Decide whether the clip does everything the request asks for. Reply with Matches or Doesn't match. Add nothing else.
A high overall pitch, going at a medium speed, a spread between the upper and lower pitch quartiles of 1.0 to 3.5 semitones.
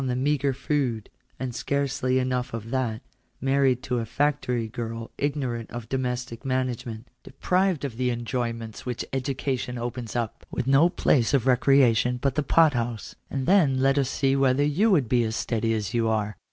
Doesn't match